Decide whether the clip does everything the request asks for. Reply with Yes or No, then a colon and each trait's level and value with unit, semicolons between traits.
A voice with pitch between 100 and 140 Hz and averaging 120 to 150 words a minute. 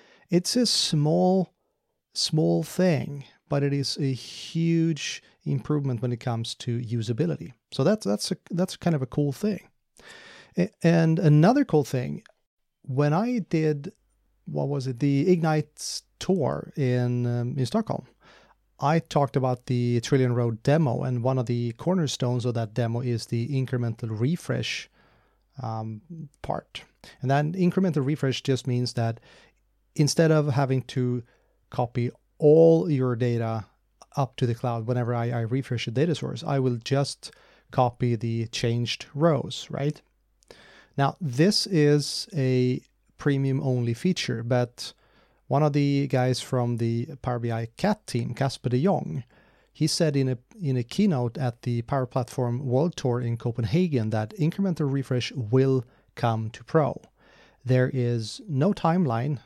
Yes: low, 135 Hz; average, 145 wpm